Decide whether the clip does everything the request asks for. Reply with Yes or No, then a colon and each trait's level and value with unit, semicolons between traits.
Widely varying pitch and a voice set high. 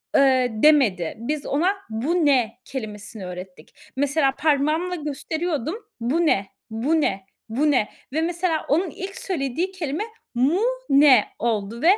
Yes: wide, 5.8 semitones; very high, 280 Hz